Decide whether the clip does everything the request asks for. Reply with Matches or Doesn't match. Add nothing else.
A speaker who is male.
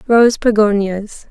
Doesn't match